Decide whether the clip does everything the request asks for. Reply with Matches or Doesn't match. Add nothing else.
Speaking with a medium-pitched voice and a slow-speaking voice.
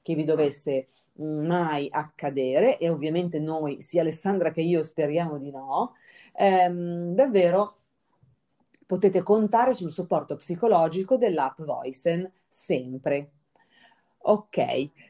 Matches